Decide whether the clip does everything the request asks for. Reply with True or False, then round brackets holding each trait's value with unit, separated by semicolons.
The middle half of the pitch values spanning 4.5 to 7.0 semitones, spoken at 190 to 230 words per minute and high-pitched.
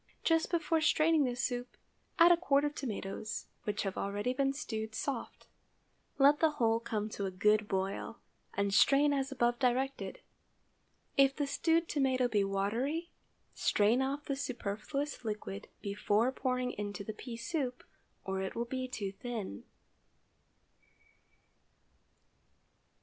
False (5.0 semitones; 135 wpm; 245 Hz)